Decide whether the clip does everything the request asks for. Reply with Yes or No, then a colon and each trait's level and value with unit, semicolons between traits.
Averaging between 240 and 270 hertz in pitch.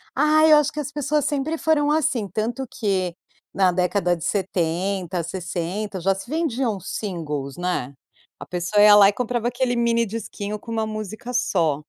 No: high, 210 Hz